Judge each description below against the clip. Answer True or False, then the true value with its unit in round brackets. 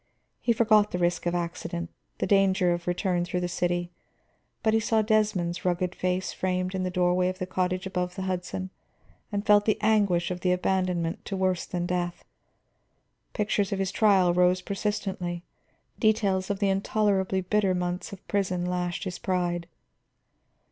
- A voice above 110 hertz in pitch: True (185 Hz)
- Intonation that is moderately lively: False (2.0 semitones)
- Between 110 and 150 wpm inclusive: False (170 wpm)